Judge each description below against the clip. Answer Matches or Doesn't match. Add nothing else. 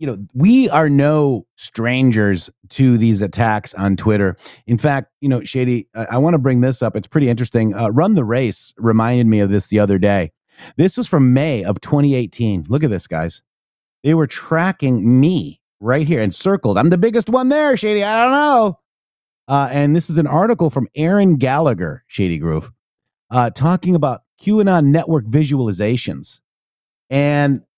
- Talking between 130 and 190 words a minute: Matches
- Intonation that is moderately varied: Doesn't match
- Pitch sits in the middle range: Doesn't match